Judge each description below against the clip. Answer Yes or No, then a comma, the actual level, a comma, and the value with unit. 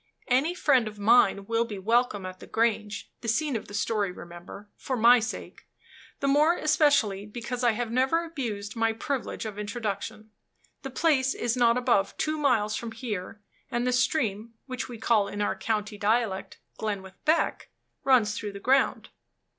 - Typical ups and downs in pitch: Yes, average, 3.5 semitones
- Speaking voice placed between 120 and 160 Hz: No, high, 230 Hz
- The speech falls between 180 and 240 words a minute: No, average, 170 wpm